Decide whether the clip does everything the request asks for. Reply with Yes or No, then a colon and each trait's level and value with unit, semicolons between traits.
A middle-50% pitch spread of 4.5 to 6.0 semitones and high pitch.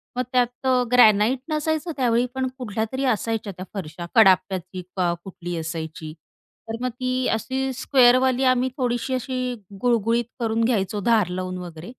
Yes: average, 5.2 semitones; high, 230 Hz